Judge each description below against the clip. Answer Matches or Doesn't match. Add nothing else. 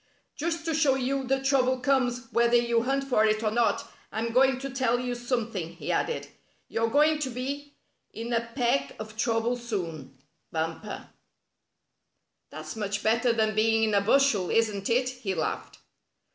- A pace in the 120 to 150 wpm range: Doesn't match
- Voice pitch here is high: Matches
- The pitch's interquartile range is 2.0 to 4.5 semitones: Matches